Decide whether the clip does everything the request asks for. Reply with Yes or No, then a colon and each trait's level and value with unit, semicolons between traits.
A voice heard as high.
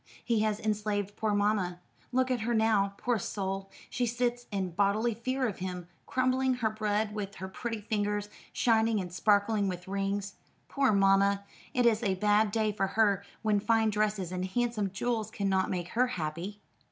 Yes: high, 210 Hz